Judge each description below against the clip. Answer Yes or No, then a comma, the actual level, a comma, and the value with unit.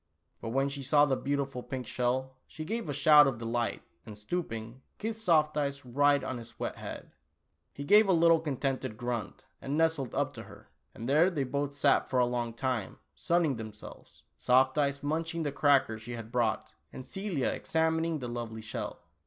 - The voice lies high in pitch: No, low, 135 Hz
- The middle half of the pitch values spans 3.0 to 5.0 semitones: Yes, average, 4.0 semitones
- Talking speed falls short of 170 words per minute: No, average, 190 wpm